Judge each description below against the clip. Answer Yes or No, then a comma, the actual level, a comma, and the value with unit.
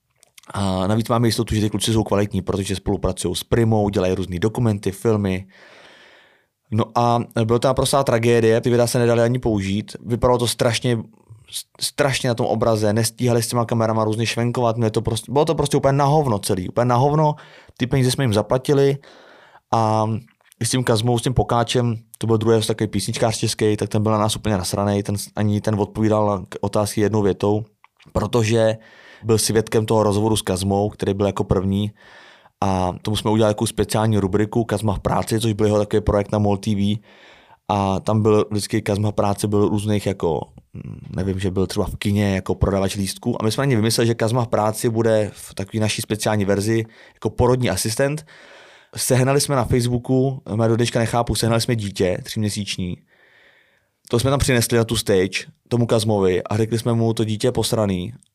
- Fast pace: Yes, fast, 190 wpm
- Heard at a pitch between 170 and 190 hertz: No, low, 110 Hz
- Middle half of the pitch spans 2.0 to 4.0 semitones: Yes, narrow, 2.5 semitones